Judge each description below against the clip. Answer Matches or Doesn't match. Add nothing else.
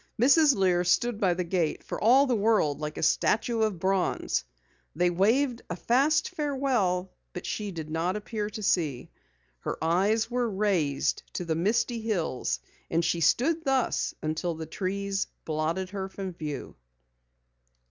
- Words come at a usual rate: Matches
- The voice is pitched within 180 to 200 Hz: Matches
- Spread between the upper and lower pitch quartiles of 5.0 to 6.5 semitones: Matches